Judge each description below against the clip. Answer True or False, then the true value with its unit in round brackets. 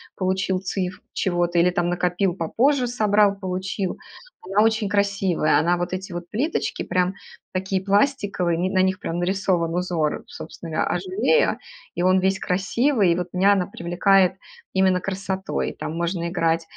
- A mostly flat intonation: True (2.2 semitones)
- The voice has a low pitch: False (185 Hz)